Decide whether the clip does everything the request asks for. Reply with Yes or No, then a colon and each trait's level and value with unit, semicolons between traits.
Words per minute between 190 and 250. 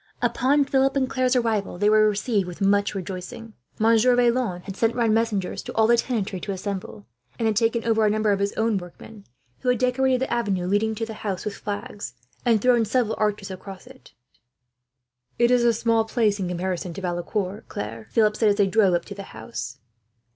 Yes: average, 200 wpm